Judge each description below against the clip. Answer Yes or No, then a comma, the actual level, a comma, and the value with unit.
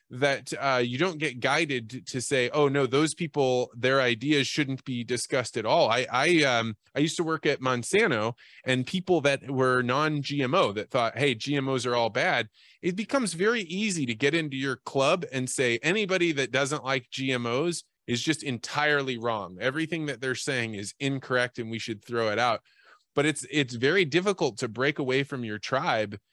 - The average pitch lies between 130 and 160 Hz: Yes, low, 135 Hz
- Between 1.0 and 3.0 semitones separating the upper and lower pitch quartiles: No, average, 3.4 semitones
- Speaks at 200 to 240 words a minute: No, average, 190 wpm